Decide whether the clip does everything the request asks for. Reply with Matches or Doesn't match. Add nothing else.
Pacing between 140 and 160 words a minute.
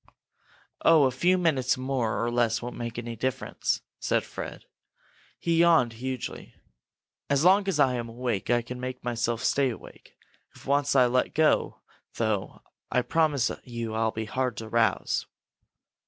Matches